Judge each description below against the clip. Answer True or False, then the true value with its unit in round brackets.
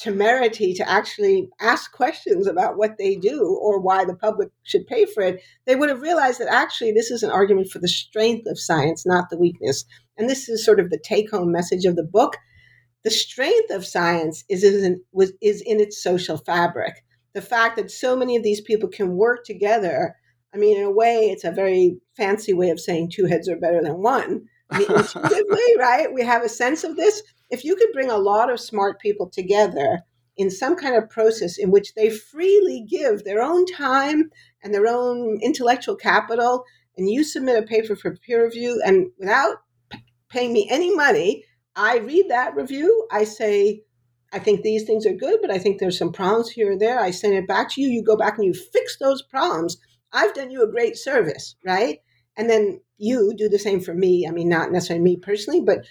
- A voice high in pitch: True (215 Hz)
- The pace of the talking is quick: True (215 wpm)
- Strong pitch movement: True (6.7 semitones)